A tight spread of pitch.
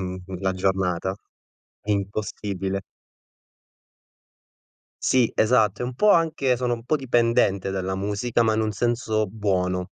No: average, 3.9 semitones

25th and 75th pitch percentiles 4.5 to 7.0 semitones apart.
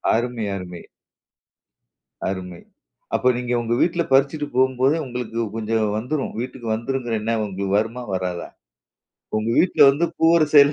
No: average, 3.7 semitones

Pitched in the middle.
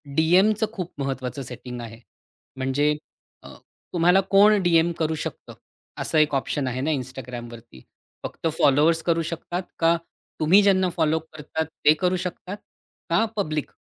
Yes: medium, 160 Hz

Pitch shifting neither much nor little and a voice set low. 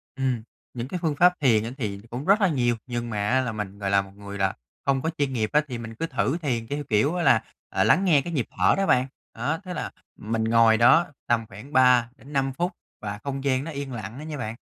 Yes: average, 4.5 semitones; low, 125 Hz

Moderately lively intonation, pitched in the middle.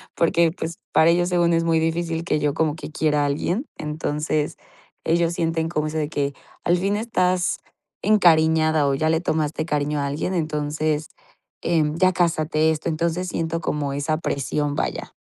No: narrow, 2.0 semitones; medium, 160 Hz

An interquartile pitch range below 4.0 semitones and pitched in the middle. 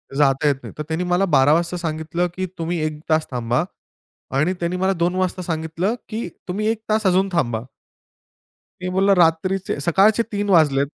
Yes: average, 3.4 semitones; medium, 175 Hz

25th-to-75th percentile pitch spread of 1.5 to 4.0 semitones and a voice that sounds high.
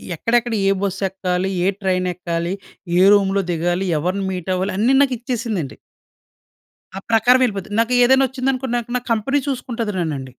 No: average, 4.9 semitones; high, 200 Hz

